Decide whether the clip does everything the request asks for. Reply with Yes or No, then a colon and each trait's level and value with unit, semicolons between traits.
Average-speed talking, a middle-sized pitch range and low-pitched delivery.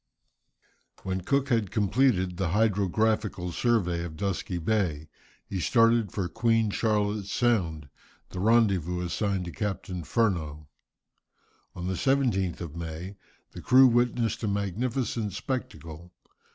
No: slow, 120 wpm; average, 4.4 semitones; low, 100 Hz